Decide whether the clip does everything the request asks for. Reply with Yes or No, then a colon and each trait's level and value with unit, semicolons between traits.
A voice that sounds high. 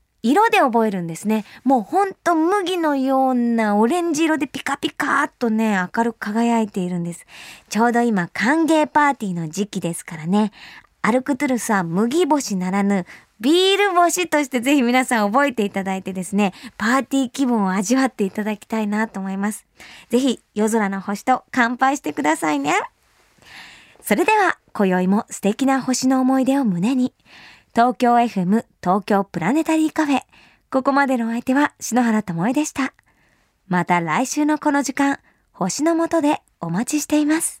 Yes: high, 240 Hz